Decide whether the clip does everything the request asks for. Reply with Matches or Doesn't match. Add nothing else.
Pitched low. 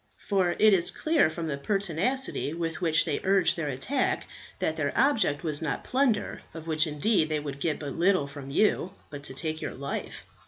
Doesn't match